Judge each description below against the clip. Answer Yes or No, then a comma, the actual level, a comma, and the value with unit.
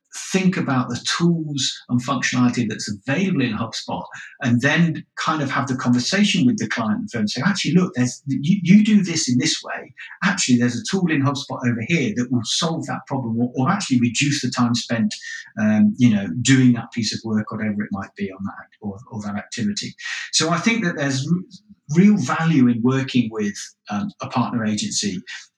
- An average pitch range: No, wide, 6.9 semitones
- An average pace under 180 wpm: No, average, 200 wpm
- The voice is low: Yes, low, 130 Hz